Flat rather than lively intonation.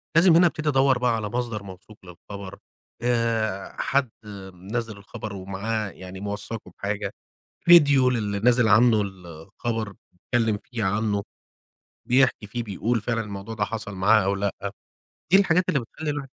No: average, 3.5 semitones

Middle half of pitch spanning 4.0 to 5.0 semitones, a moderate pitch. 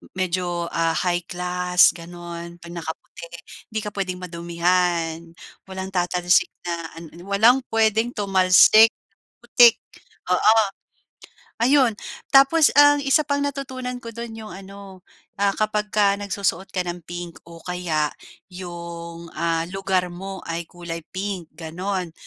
No: average, 3.3 semitones; medium, 180 Hz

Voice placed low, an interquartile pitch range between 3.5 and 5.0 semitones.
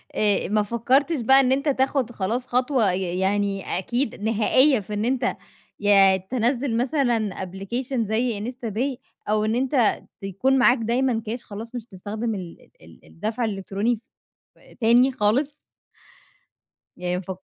No: high, 225 Hz; average, 3.9 semitones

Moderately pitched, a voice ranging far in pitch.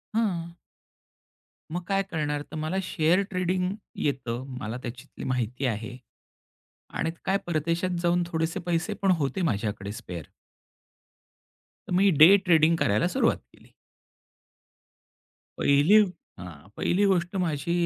Yes: medium, 165 Hz; wide, 6.1 semitones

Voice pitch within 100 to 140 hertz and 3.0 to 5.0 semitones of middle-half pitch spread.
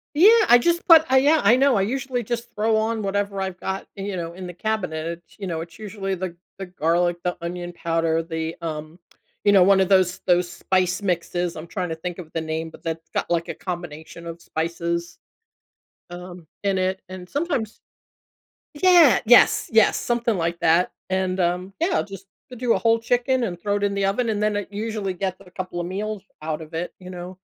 No: medium, 185 Hz; average, 4.0 semitones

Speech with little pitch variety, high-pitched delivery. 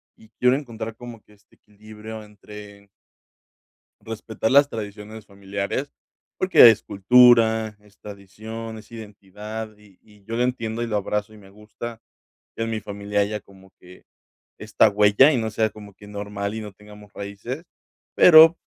No: narrow, 1.8 semitones; low, 105 Hz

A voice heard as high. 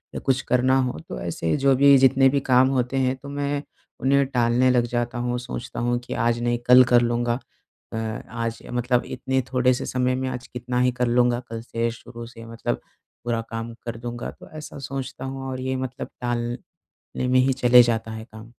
No: low, 125 Hz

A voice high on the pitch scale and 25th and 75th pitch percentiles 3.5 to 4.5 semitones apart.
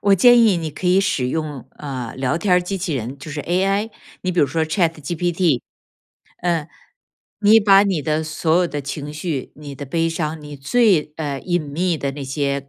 No: medium, 160 Hz; average, 4.0 semitones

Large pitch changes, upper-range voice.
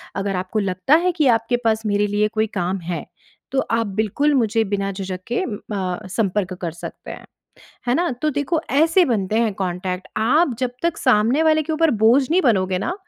Yes: wide, 6.5 semitones; high, 220 Hz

